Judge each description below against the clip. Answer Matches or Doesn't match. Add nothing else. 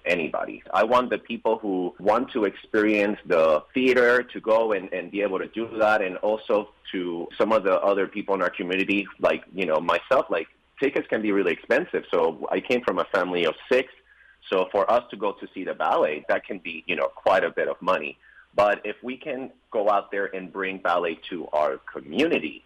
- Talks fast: Matches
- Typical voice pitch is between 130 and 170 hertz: Doesn't match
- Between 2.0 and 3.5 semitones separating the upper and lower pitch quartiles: Doesn't match